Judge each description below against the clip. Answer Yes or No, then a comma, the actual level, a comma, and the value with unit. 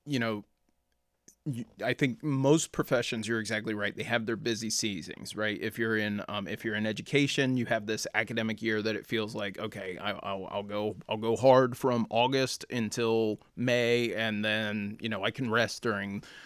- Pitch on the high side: No, low, 110 Hz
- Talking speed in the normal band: Yes, average, 190 wpm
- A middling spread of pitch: No, narrow, 2.3 semitones